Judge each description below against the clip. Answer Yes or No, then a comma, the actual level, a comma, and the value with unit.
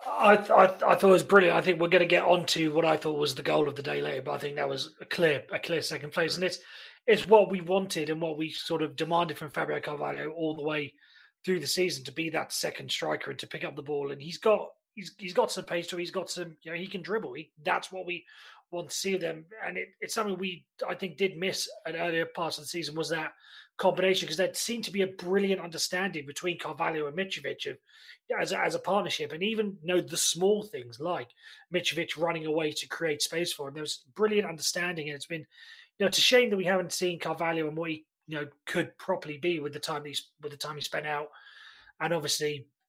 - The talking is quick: Yes, fast, 255 wpm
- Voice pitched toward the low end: No, medium, 170 Hz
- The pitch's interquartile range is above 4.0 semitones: No, average, 3.3 semitones